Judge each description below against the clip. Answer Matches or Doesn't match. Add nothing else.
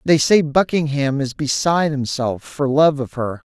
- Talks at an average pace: Matches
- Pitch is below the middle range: Doesn't match